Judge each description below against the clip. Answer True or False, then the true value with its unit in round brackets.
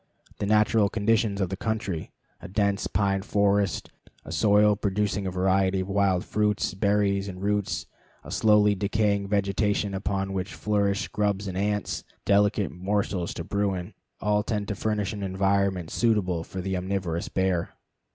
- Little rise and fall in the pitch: True (1.5 semitones)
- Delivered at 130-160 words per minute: True (150 wpm)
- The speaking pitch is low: True (100 Hz)